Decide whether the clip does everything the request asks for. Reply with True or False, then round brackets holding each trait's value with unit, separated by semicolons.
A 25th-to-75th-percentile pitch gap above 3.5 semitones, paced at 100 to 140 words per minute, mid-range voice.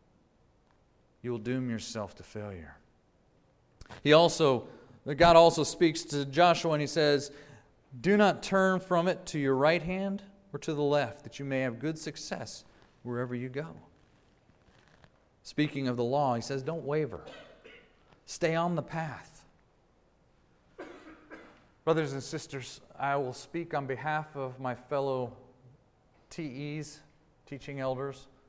True (3.9 semitones; 135 wpm; 145 Hz)